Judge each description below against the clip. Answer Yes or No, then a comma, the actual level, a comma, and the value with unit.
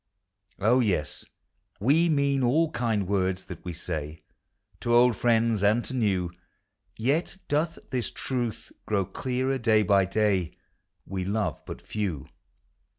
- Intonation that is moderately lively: Yes, average, 4.9 semitones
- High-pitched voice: No, low, 110 Hz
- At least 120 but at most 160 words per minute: Yes, average, 145 wpm